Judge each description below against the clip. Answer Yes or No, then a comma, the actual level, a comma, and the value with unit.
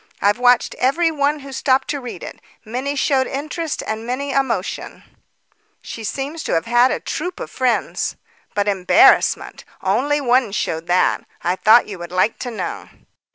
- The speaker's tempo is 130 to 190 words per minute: Yes, average, 165 wpm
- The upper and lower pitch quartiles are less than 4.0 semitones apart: No, average, 4.8 semitones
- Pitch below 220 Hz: No, very high, 250 Hz